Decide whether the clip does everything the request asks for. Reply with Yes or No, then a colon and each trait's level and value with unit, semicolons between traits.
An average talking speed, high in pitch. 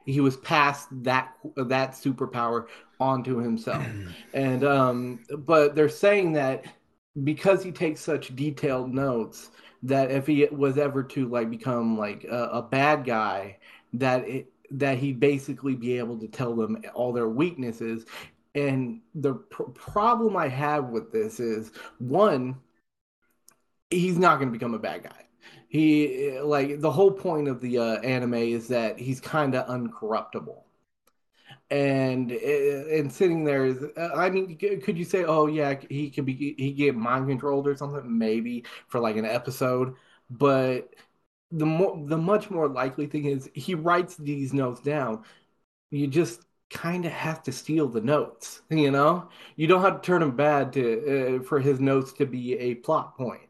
No: average, 165 wpm; medium, 140 Hz